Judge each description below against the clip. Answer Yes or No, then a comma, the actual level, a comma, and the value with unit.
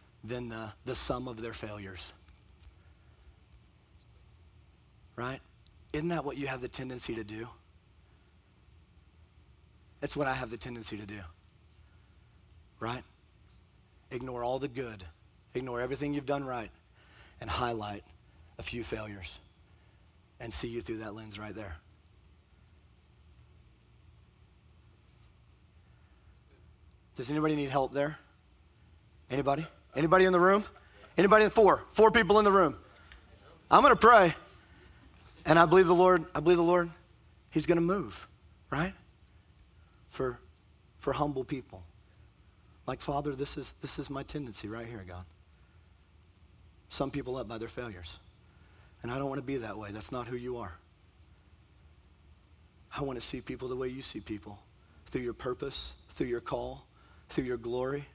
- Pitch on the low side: Yes, low, 105 Hz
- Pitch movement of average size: No, wide, 6.9 semitones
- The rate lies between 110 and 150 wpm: Yes, average, 140 wpm